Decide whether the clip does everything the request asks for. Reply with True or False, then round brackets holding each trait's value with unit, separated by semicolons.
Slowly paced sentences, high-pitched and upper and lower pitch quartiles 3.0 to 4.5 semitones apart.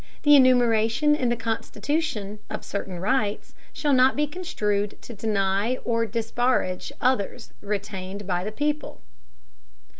True (125 wpm; 225 Hz; 4.2 semitones)